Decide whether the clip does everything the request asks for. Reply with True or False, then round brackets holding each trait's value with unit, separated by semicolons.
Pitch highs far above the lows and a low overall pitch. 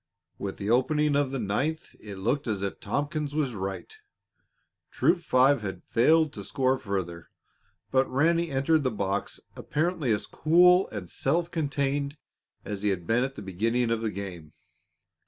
True (6.6 semitones; 130 Hz)